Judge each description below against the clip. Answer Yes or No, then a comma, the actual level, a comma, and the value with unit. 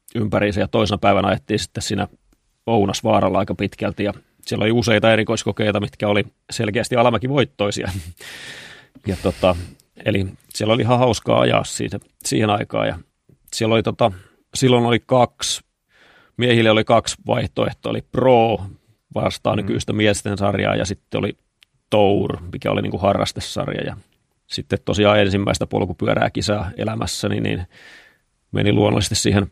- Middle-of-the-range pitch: No, low, 105 Hz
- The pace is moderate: Yes, average, 135 wpm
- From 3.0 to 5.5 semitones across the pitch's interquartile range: No, narrow, 2.4 semitones